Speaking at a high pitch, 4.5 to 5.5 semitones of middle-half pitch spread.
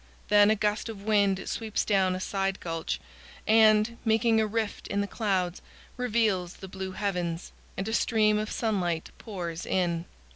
No: high, 205 Hz; average, 2.8 semitones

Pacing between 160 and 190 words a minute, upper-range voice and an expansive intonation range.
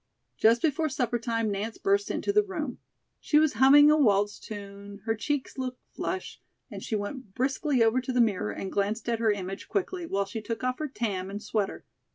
No: fast, 205 wpm; high, 235 Hz; wide, 5.9 semitones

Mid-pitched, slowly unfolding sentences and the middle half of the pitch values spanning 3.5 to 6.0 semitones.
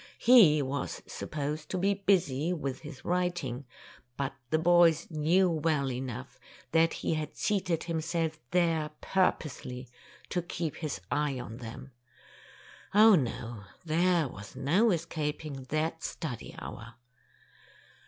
Yes: medium, 155 Hz; slow, 125 wpm; average, 4.1 semitones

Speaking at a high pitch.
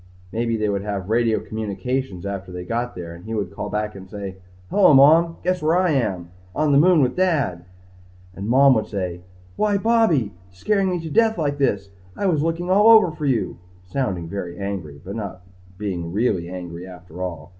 No: low, 110 Hz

